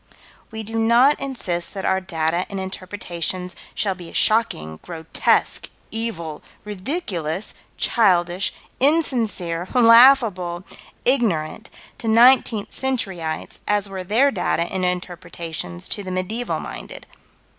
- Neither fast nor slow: No, slow, 115 wpm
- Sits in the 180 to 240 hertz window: Yes, high, 190 Hz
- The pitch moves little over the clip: No, average, 4.8 semitones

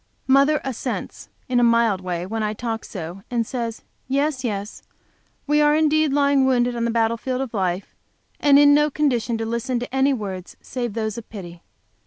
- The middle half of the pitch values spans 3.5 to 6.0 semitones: Yes, average, 4.0 semitones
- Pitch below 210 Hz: No, high, 240 Hz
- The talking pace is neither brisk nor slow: Yes, average, 190 wpm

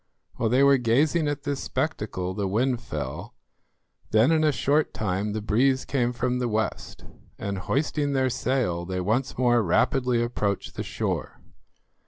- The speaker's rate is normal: Yes, average, 160 wpm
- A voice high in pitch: No, low, 125 Hz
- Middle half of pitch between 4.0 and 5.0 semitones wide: Yes, average, 4.3 semitones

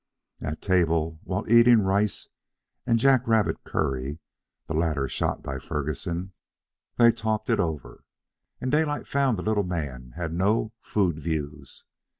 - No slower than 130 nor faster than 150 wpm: Yes, average, 140 wpm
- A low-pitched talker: Yes, very low, 90 Hz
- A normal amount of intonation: No, wide, 6.2 semitones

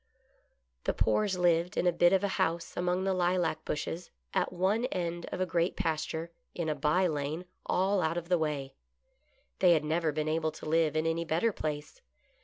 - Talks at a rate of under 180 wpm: No, average, 195 wpm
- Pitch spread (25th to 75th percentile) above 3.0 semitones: No, narrow, 2.5 semitones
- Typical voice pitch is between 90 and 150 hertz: No, medium, 170 Hz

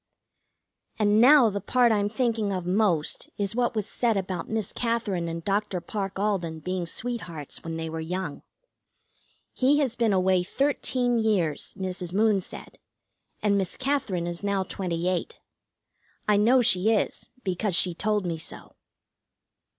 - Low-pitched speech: No, high, 200 Hz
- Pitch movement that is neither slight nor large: Yes, average, 3.8 semitones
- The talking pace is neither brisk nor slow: Yes, average, 150 wpm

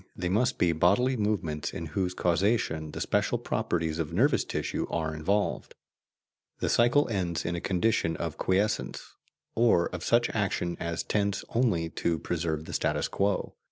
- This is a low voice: Yes, very low, 90 Hz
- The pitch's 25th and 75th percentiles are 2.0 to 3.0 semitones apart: No, average, 4.4 semitones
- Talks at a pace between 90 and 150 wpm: No, average, 160 wpm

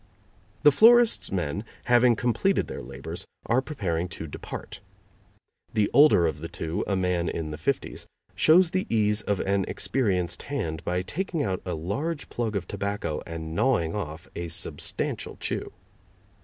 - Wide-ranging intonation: Yes, wide, 7.2 semitones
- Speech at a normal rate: Yes, average, 155 wpm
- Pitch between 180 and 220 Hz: No, low, 100 Hz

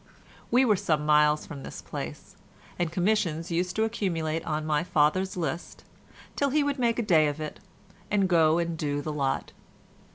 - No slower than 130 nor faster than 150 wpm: No, average, 175 wpm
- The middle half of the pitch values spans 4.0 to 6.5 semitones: Yes, average, 4.5 semitones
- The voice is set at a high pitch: No, medium, 165 Hz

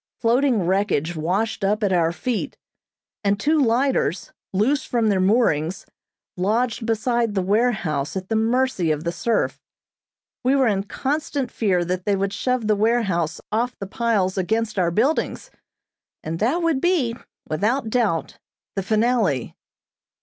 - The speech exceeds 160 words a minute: No, average, 145 wpm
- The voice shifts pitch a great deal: No, average, 4.7 semitones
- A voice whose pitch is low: No, high, 215 Hz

